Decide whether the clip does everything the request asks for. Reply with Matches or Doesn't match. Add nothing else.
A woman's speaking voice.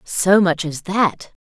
Matches